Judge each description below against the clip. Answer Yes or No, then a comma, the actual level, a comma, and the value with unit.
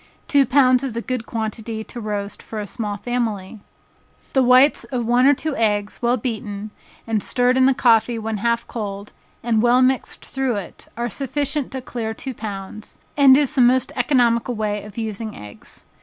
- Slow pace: No, average, 185 wpm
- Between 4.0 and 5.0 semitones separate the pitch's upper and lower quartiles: No, average, 3.0 semitones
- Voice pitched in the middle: No, high, 235 Hz